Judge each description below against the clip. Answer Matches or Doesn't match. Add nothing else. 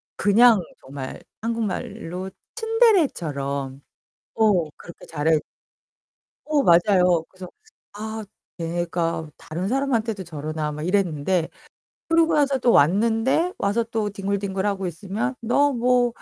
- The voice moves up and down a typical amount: Doesn't match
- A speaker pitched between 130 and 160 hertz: Doesn't match